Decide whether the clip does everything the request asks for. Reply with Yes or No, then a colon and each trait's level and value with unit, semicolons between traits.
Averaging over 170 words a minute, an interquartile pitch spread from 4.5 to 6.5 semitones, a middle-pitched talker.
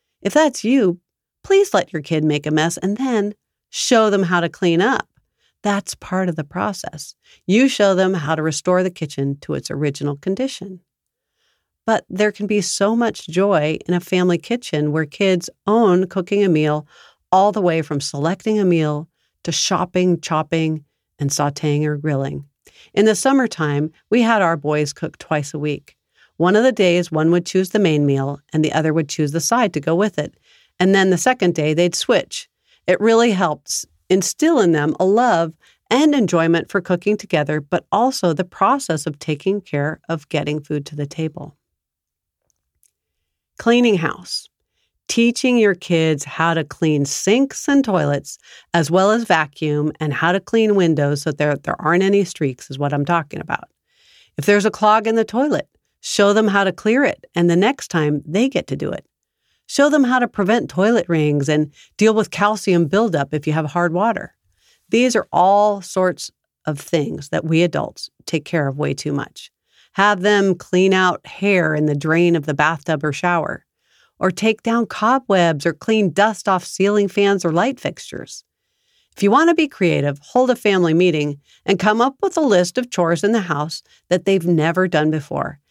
Yes: average, 190 wpm; average, 5.2 semitones; medium, 175 Hz